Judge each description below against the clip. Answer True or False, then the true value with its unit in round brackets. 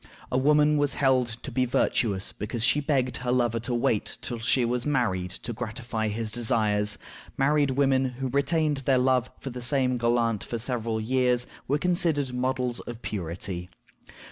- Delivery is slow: False (170 wpm)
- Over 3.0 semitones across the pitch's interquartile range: False (2.6 semitones)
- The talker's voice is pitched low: True (125 Hz)